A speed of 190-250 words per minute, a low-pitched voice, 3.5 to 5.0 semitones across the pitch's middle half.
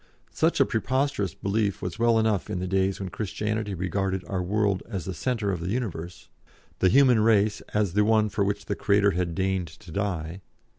No: average, 195 wpm; low, 100 Hz; average, 2.8 semitones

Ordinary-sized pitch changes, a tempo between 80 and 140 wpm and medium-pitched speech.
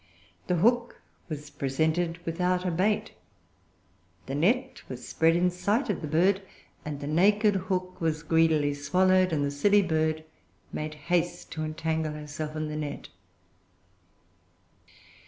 Yes: average, 3.4 semitones; slow, 135 wpm; medium, 165 Hz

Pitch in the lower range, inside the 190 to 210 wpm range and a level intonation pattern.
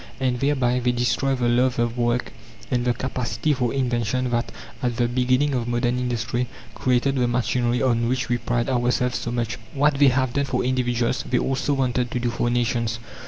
Yes: low, 125 Hz; average, 195 wpm; narrow, 1.2 semitones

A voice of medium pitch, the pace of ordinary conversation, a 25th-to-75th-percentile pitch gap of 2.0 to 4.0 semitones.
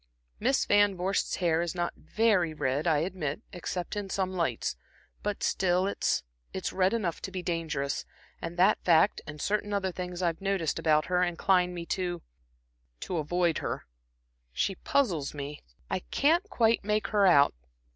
Yes: medium, 180 Hz; average, 165 wpm; average, 3.2 semitones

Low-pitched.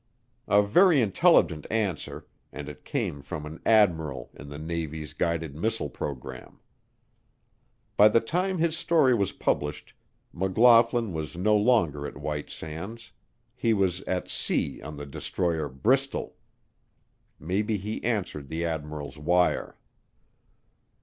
Yes: very low, 90 Hz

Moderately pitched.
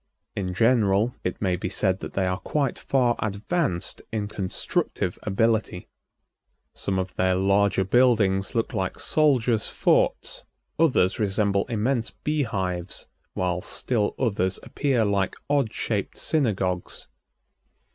No: low, 100 Hz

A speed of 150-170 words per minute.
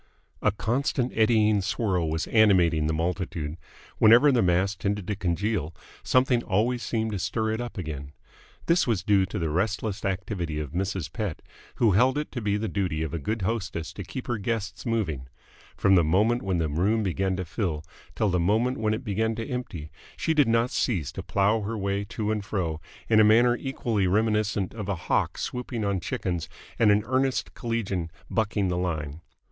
No: average, 190 wpm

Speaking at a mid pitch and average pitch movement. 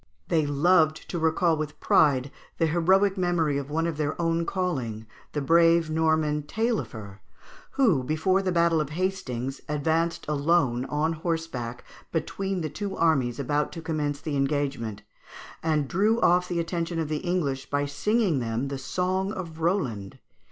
Yes: medium, 160 Hz; average, 3.5 semitones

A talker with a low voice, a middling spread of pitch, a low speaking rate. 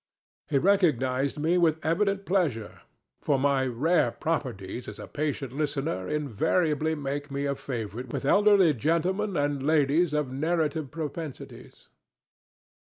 No: medium, 150 Hz; average, 3.5 semitones; slow, 125 wpm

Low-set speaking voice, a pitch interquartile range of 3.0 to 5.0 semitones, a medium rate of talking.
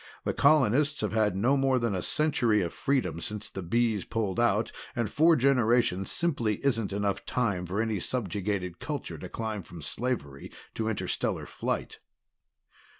Yes: low, 110 Hz; average, 4.6 semitones; average, 155 wpm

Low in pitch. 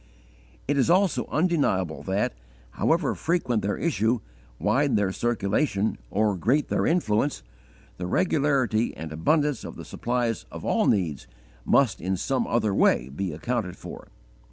Yes: low, 115 Hz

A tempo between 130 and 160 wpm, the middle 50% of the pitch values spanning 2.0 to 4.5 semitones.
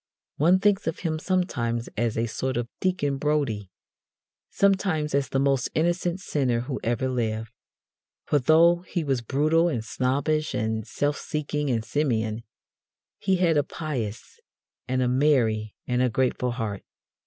No: average, 150 wpm; average, 5.1 semitones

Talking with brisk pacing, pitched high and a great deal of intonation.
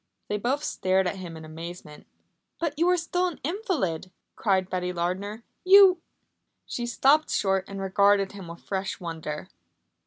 No: average, 160 wpm; high, 195 Hz; wide, 8.4 semitones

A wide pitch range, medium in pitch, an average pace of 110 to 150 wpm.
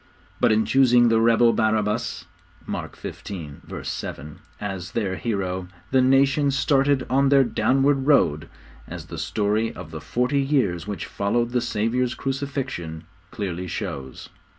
No: wide, 5.8 semitones; low, 115 Hz; slow, 135 wpm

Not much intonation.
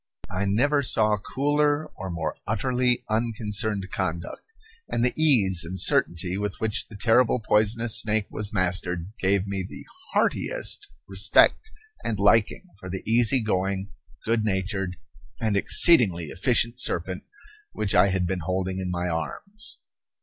No: average, 3.8 semitones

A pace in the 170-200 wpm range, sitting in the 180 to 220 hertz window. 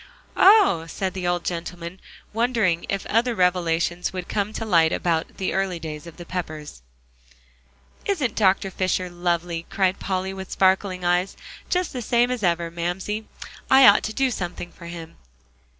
No: average, 160 wpm; medium, 185 Hz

